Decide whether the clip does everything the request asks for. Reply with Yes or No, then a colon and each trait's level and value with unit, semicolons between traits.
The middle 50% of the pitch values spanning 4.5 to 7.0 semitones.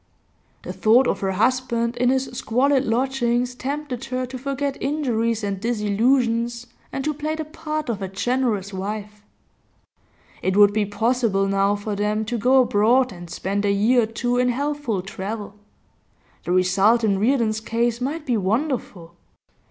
No: average, 3.9 semitones